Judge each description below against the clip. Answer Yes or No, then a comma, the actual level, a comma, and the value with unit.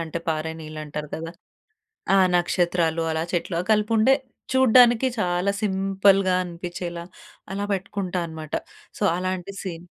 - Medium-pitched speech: Yes, medium, 180 Hz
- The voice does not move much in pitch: No, average, 3.1 semitones